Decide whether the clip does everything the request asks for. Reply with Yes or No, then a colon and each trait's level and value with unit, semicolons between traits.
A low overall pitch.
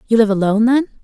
No: high, 225 Hz